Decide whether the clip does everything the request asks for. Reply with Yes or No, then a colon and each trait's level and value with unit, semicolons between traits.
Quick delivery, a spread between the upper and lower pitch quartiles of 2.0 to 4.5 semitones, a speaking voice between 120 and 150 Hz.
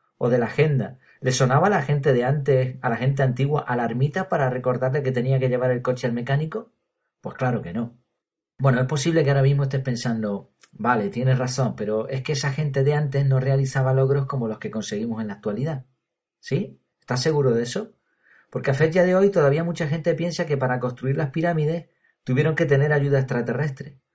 Yes: fast, 205 wpm; average, 2.9 semitones; low, 135 Hz